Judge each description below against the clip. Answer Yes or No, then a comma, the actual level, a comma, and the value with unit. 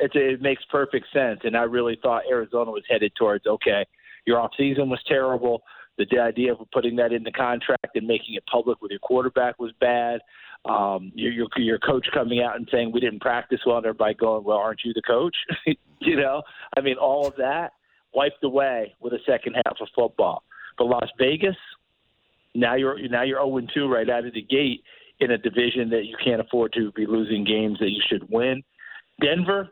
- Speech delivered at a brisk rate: Yes, fast, 210 wpm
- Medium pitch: No, low, 120 Hz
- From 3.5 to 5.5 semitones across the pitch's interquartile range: No, average, 2.7 semitones